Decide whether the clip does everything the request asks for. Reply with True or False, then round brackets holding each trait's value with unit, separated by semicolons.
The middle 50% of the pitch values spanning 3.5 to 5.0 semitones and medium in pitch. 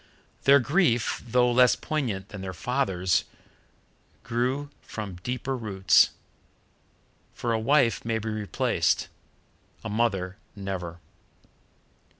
False (4.4 semitones; 115 Hz)